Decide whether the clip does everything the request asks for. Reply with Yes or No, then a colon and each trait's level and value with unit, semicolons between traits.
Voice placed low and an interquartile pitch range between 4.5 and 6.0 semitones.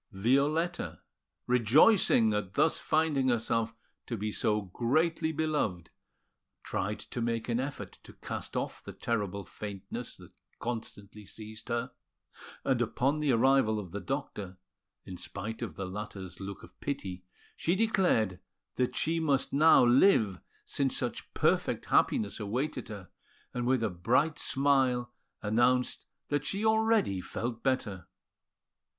Yes: low, 120 Hz; average, 5.1 semitones